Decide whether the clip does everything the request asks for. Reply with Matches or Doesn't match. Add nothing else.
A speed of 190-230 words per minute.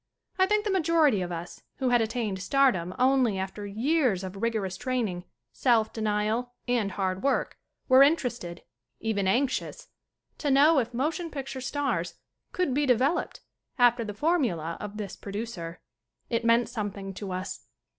Doesn't match